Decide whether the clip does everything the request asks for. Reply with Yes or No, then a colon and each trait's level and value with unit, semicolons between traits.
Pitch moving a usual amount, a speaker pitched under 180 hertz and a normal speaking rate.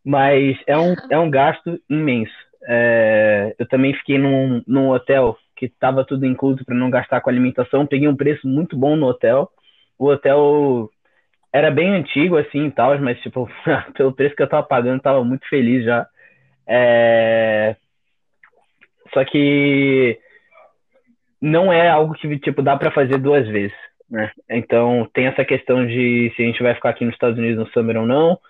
Yes: average, 3.1 semitones; low, 135 Hz; average, 175 wpm